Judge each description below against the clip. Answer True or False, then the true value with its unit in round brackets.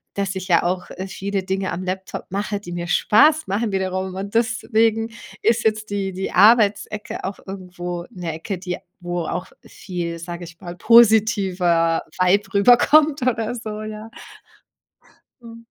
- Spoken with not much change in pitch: False (3.4 semitones)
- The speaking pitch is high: True (195 Hz)